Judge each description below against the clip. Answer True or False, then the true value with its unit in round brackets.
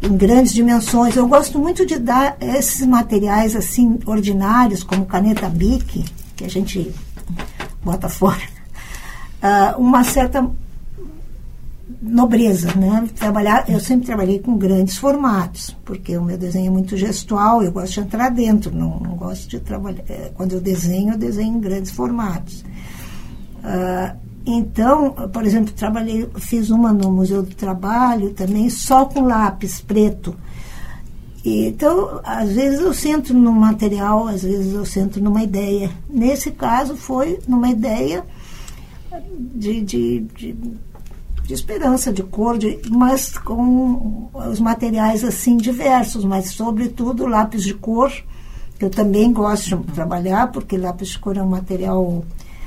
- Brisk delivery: False (140 wpm)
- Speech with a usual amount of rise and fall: True (4.1 semitones)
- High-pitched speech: True (215 Hz)